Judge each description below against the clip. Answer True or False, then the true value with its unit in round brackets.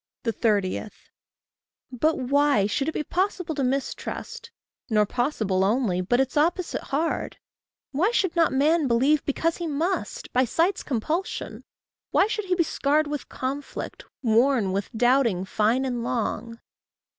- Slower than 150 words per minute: True (140 wpm)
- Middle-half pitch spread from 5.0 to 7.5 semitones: True (5.5 semitones)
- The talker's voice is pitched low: False (270 Hz)